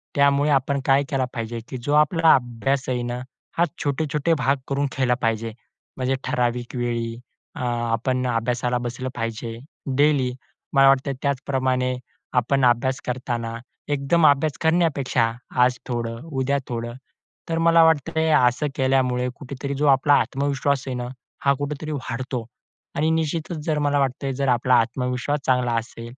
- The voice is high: No, low, 130 Hz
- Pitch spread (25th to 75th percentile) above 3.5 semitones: No, average, 2.7 semitones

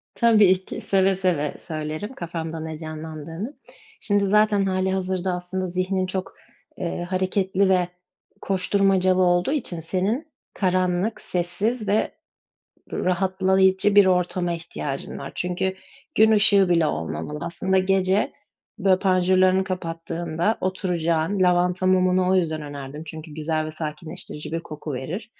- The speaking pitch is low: No, medium, 185 Hz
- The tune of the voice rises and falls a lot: No, narrow, 2.5 semitones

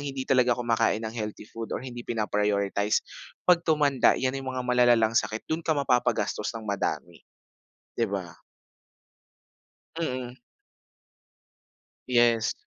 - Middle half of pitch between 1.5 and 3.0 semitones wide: No, average, 3.4 semitones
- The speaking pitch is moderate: No, low, 120 Hz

